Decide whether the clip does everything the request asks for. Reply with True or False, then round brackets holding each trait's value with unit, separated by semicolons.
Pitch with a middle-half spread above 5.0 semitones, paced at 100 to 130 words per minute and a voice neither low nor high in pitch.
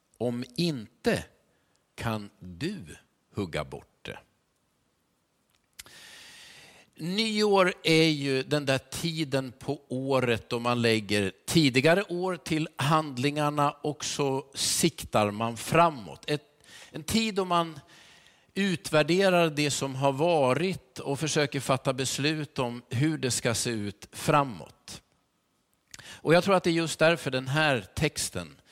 False (4.5 semitones; 125 wpm; 145 Hz)